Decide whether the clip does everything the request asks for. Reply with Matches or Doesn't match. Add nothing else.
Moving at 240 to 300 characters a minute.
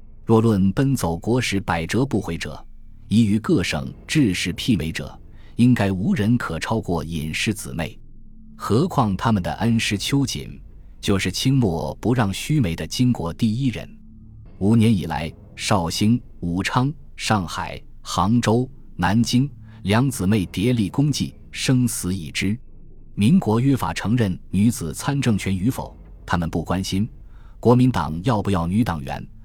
Doesn't match